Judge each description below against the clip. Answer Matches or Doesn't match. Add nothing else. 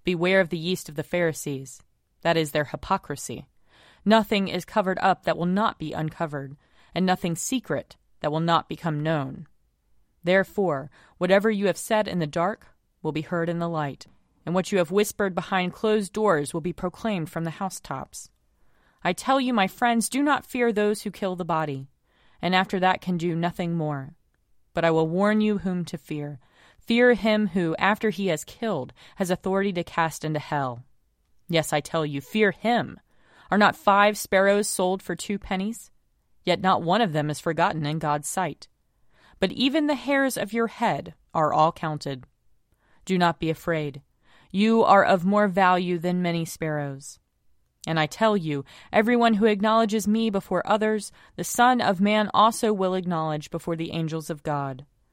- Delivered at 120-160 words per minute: Doesn't match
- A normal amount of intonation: Matches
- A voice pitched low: Doesn't match